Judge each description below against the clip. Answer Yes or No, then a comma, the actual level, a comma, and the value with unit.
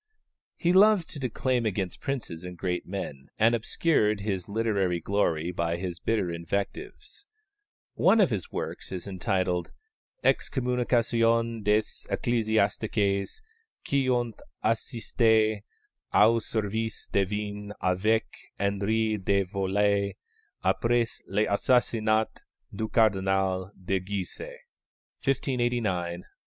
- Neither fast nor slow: No, slow, 105 wpm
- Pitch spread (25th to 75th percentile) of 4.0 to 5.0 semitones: No, average, 3.3 semitones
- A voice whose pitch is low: Yes, low, 105 Hz